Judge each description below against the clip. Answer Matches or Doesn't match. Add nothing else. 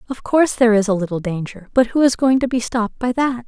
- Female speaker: Matches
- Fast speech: Matches